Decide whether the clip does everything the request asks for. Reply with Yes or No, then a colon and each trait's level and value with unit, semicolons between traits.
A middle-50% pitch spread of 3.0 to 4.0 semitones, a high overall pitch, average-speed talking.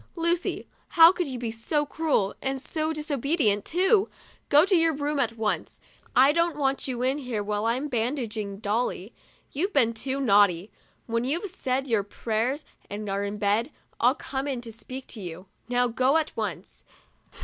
No: average, 5.1 semitones; very high, 255 Hz; average, 175 wpm